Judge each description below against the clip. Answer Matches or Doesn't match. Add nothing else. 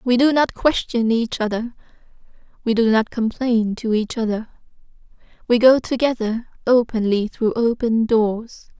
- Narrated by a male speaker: Doesn't match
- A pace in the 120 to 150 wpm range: Matches